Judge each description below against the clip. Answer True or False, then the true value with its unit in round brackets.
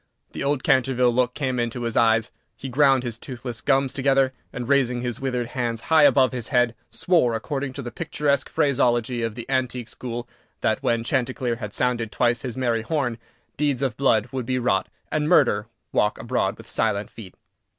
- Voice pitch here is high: False (125 Hz)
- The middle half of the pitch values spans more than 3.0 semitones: False (2.4 semitones)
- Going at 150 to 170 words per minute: False (185 wpm)